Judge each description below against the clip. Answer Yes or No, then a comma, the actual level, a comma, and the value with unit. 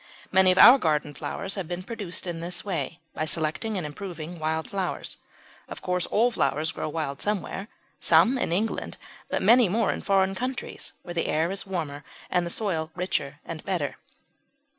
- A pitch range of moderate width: Yes, average, 3.8 semitones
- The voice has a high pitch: No, medium, 180 Hz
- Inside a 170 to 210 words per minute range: Yes, average, 180 wpm